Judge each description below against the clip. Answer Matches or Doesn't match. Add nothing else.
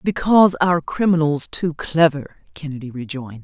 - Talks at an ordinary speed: Doesn't match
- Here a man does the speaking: Doesn't match